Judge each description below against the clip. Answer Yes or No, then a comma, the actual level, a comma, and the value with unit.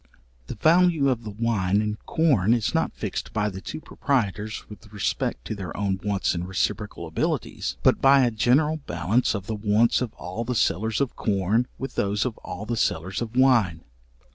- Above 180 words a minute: Yes, average, 190 wpm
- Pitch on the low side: Yes, low, 110 Hz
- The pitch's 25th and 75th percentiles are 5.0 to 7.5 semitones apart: No, average, 3.9 semitones